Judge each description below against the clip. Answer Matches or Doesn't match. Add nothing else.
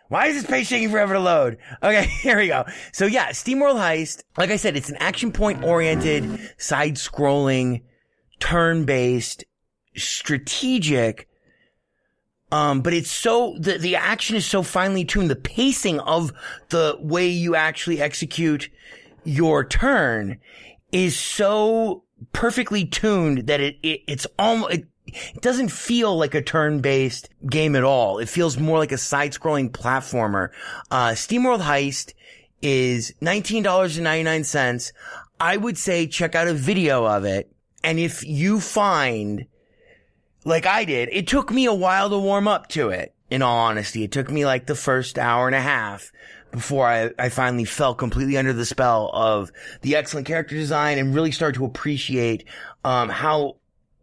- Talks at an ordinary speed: Matches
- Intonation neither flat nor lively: Doesn't match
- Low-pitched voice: Doesn't match